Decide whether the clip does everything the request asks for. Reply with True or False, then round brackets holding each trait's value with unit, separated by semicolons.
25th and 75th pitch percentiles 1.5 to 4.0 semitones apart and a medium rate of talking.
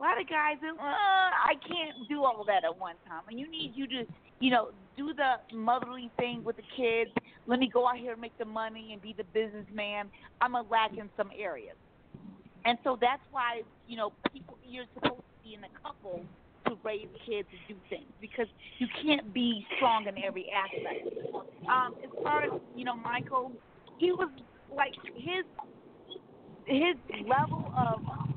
False (4.4 semitones; 190 wpm)